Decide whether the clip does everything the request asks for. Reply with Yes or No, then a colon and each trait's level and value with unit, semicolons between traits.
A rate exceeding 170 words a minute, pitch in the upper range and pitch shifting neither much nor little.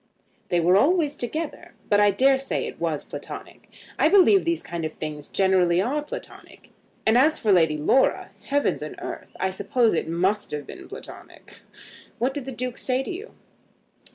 No: average, 180 wpm; high, 230 Hz; wide, 7.8 semitones